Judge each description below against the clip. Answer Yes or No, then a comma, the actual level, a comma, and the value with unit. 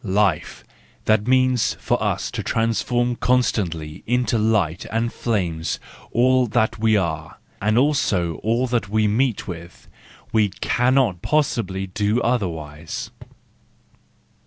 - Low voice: Yes, low, 110 Hz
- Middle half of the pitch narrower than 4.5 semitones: No, average, 4.8 semitones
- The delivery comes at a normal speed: No, slow, 110 wpm